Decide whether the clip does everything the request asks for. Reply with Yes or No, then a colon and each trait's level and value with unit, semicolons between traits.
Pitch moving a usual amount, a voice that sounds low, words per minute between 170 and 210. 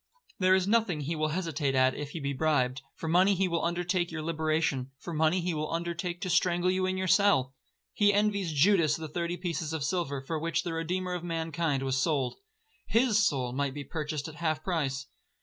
No: average, 3.5 semitones; medium, 165 Hz; average, 200 wpm